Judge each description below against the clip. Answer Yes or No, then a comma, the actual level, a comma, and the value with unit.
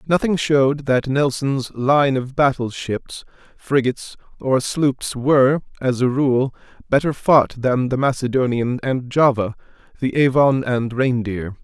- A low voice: Yes, low, 130 Hz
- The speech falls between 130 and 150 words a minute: Yes, slow, 135 wpm